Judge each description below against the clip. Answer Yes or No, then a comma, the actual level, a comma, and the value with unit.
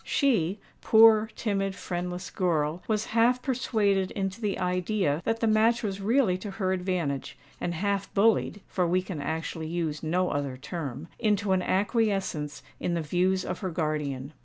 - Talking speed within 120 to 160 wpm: Yes, average, 155 wpm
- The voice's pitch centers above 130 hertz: Yes, medium, 185 Hz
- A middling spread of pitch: Yes, average, 4.1 semitones